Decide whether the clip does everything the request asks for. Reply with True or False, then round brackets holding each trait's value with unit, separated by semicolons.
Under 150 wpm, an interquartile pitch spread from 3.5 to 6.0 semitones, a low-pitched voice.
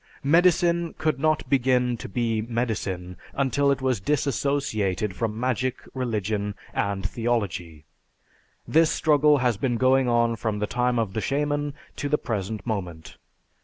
True (140 wpm; 4.8 semitones; 120 Hz)